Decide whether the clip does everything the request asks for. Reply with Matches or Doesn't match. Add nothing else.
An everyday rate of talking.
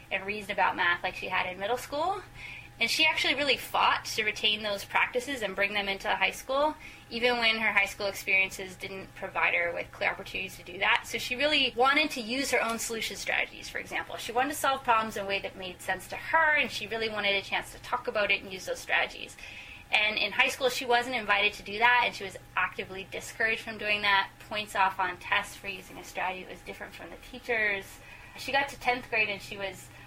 Doesn't match